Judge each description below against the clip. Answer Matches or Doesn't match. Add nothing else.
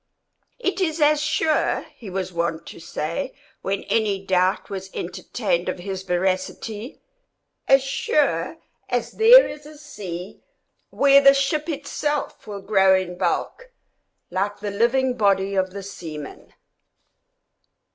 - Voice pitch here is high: Matches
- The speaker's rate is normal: Doesn't match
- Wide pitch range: Matches